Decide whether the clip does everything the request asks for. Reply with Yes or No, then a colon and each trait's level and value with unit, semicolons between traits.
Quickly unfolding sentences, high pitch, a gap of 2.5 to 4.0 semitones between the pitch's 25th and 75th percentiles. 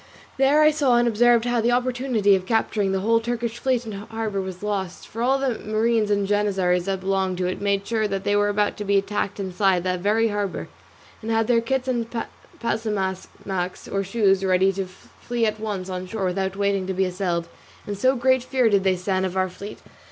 Yes: fast, 210 wpm; high, 205 Hz; average, 3.2 semitones